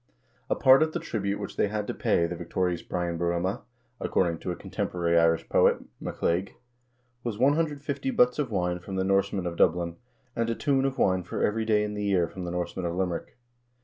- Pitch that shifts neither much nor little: Yes, average, 4.5 semitones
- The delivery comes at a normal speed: No, fast, 215 wpm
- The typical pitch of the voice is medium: No, very low, 95 Hz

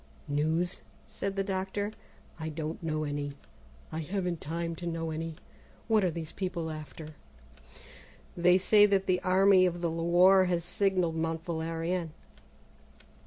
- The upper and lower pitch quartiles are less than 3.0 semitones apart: Yes, narrow, 2.6 semitones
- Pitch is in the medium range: Yes, medium, 170 Hz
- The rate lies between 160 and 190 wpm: No, average, 140 wpm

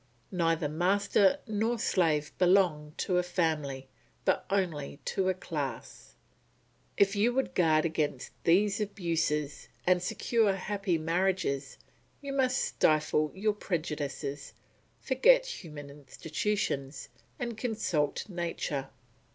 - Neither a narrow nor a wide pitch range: Yes, average, 5.0 semitones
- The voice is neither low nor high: Yes, medium, 175 Hz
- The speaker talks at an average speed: No, slow, 110 wpm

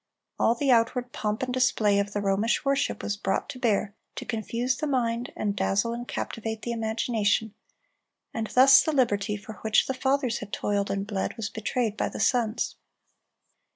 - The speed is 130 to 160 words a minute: No, average, 180 wpm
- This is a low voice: No, high, 225 Hz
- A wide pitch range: No, average, 3.3 semitones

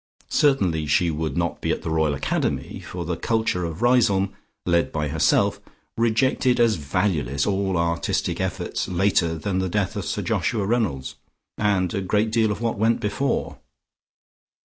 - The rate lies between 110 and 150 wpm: No, average, 160 wpm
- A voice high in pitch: No, very low, 95 Hz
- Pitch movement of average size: Yes, average, 5.0 semitones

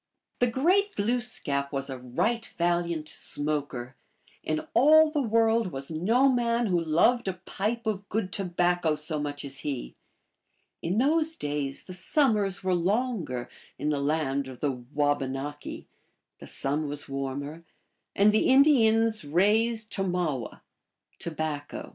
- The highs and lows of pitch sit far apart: Yes, wide, 7.7 semitones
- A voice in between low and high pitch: Yes, medium, 175 Hz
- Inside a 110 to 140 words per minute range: Yes, slow, 135 wpm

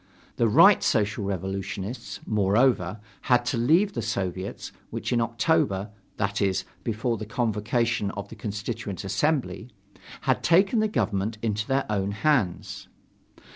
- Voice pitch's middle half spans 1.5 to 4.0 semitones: Yes, average, 3.5 semitones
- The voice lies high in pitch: No, low, 110 Hz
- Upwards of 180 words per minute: No, slow, 135 wpm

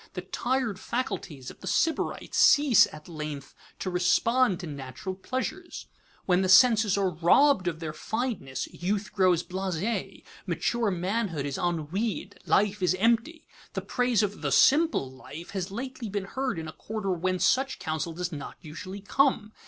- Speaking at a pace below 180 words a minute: Yes, average, 160 wpm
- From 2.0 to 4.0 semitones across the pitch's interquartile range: No, wide, 5.4 semitones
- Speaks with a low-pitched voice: No, high, 190 Hz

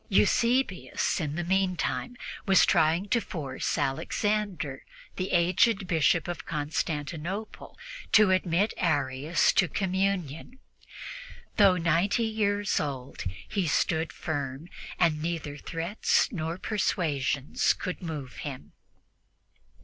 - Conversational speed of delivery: No, slow, 105 wpm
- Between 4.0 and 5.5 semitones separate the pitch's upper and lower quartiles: Yes, average, 4.5 semitones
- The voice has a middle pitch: Yes, medium, 170 Hz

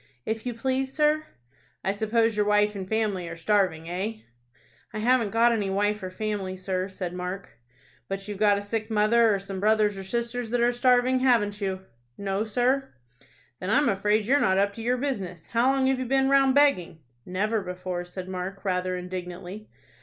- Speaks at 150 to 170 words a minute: No, average, 190 wpm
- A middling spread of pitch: Yes, average, 4.0 semitones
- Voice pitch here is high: Yes, high, 210 Hz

